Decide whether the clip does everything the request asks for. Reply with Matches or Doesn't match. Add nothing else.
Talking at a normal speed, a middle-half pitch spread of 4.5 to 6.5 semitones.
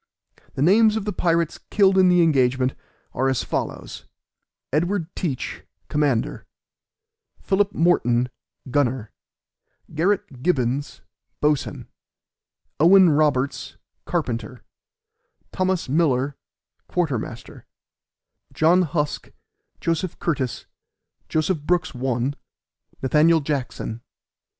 Doesn't match